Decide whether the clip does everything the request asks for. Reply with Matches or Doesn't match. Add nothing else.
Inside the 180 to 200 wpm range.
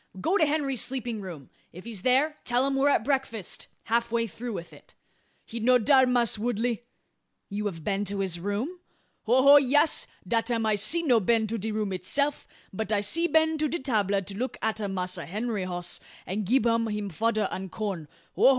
Matches